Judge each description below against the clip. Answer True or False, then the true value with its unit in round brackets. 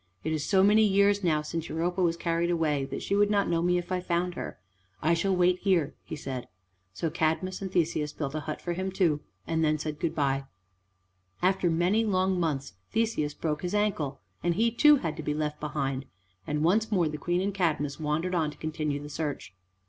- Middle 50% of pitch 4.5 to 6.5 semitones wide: False (3.6 semitones)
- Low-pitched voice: False (165 Hz)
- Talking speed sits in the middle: False (215 wpm)